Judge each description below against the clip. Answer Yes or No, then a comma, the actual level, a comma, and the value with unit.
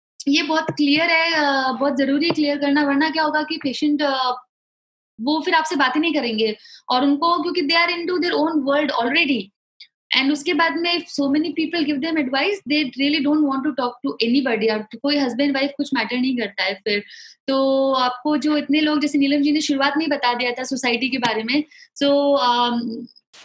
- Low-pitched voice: No, very high, 285 Hz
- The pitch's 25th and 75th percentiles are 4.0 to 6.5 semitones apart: No, average, 3.2 semitones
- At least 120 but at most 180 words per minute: No, fast, 205 wpm